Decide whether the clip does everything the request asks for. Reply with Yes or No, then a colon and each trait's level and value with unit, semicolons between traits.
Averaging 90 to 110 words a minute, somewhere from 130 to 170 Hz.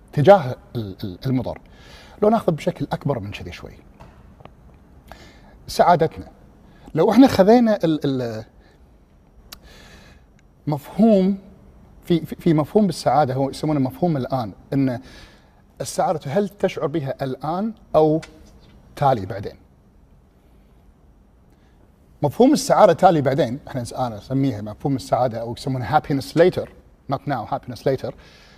Yes: average, 100 wpm; low, 135 Hz